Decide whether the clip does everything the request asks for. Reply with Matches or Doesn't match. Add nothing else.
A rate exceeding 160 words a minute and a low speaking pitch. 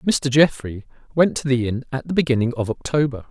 Matches